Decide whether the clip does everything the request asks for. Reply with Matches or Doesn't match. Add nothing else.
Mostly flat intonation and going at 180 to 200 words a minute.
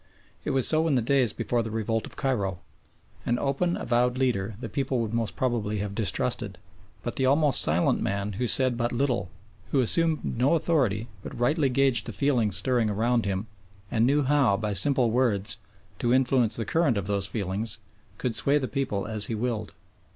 Doesn't match